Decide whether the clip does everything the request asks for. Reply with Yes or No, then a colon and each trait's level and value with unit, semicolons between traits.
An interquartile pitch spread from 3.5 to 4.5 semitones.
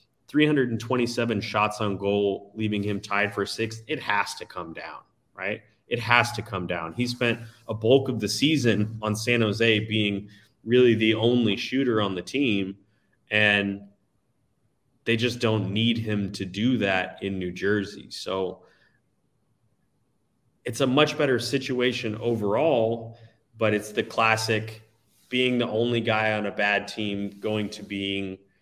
No: average, 2.7 semitones